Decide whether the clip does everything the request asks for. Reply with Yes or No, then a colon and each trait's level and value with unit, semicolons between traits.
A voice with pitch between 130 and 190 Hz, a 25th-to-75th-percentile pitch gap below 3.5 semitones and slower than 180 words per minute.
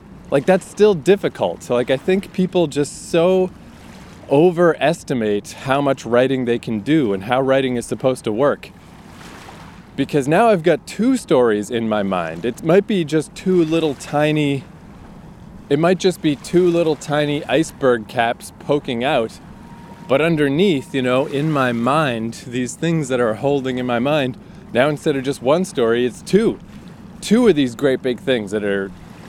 No: medium, 140 Hz; wide, 5.6 semitones; average, 170 wpm